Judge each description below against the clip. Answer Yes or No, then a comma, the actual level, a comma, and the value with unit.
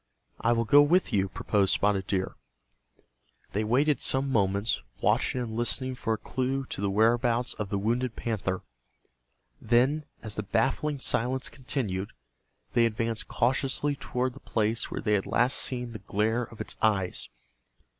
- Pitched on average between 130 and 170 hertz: No, low, 115 Hz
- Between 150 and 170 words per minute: Yes, average, 155 wpm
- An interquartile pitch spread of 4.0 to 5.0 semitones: No, average, 3.5 semitones